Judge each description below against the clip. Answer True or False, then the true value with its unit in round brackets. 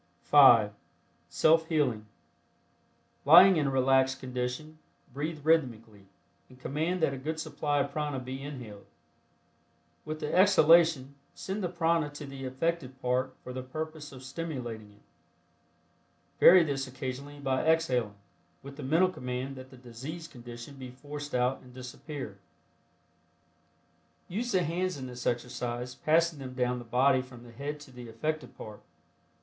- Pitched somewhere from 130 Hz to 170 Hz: True (135 Hz)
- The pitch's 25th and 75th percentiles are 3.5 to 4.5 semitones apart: True (3.8 semitones)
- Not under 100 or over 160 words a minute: True (145 wpm)